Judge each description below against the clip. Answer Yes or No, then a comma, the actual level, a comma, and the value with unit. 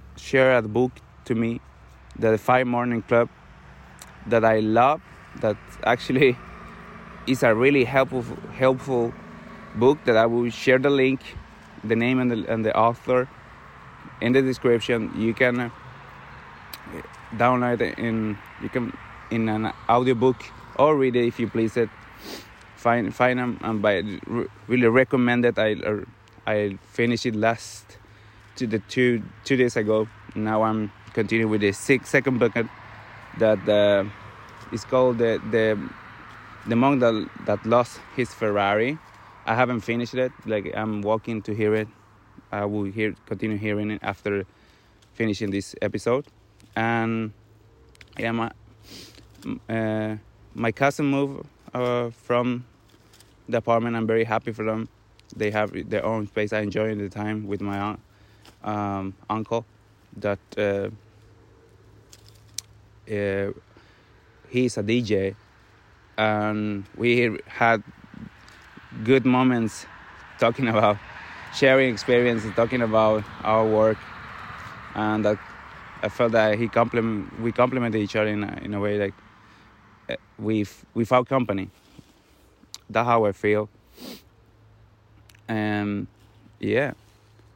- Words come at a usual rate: No, slow, 130 wpm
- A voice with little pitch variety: Yes, narrow, 2.0 semitones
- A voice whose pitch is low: Yes, low, 110 Hz